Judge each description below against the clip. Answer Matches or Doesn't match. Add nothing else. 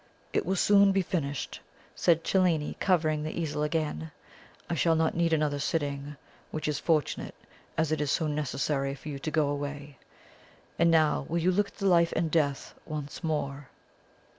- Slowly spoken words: Doesn't match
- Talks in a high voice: Doesn't match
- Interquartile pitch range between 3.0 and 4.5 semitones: Doesn't match